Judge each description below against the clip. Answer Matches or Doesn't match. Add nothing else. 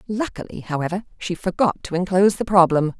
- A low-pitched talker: Doesn't match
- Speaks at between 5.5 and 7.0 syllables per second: Matches